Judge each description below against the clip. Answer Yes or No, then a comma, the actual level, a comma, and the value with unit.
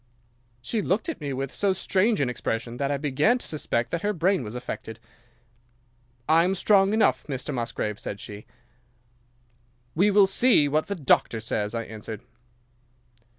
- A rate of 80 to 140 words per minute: No, average, 160 wpm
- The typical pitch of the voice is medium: Yes, medium, 145 Hz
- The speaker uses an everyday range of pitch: No, wide, 8.6 semitones